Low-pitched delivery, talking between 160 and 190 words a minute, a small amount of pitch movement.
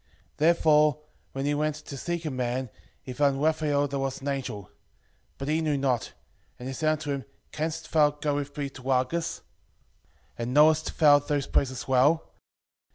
No: medium, 145 Hz; average, 180 wpm; narrow, 2.3 semitones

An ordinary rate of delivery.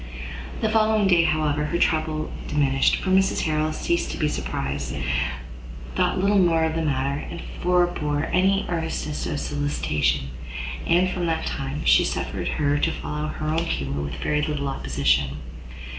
Yes: average, 160 wpm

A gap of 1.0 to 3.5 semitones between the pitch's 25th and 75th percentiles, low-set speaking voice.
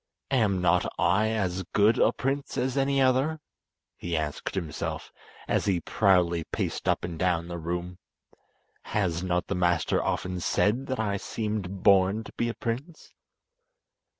No: average, 4.8 semitones; very low, 95 Hz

